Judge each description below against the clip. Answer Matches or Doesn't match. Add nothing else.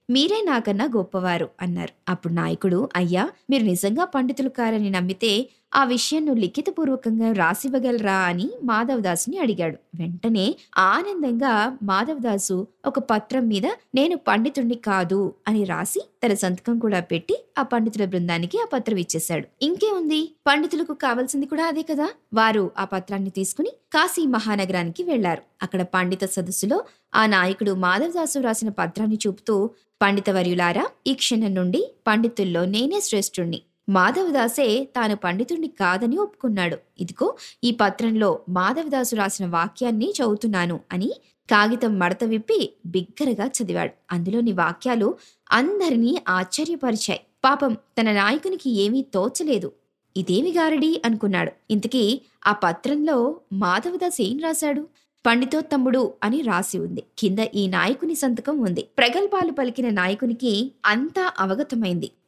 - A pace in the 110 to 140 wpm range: Matches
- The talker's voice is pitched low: Doesn't match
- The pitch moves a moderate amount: Doesn't match